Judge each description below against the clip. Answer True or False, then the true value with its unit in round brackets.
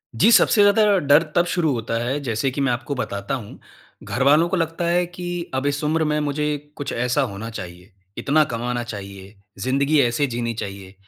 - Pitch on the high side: False (135 Hz)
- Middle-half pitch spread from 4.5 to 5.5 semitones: True (5.2 semitones)